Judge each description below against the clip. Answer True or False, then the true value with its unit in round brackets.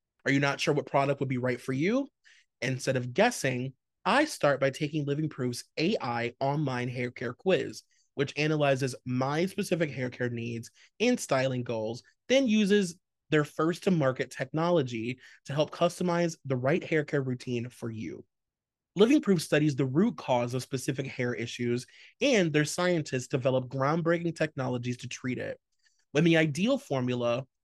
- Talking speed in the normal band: True (165 wpm)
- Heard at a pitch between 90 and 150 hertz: True (140 Hz)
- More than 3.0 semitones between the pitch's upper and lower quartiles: True (4.9 semitones)